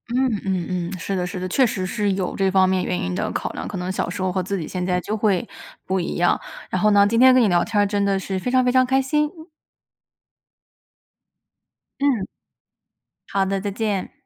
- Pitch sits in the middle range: No, high, 195 Hz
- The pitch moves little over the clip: No, average, 3.0 semitones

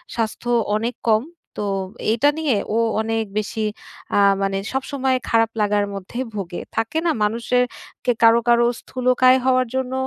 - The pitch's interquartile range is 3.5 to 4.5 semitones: No, average, 2.9 semitones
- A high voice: Yes, high, 230 Hz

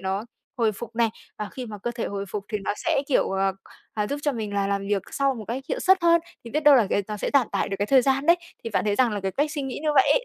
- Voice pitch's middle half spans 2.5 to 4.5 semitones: No, average, 5.3 semitones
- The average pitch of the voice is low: No, high, 230 Hz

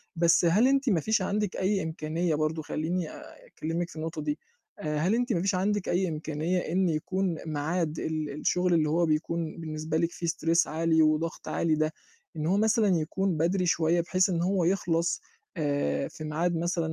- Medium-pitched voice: Yes, medium, 170 Hz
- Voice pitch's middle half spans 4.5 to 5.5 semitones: No, average, 2.8 semitones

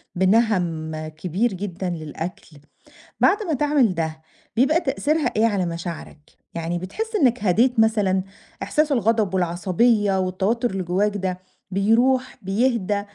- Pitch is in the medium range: No, high, 200 Hz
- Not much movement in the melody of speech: No, average, 5.0 semitones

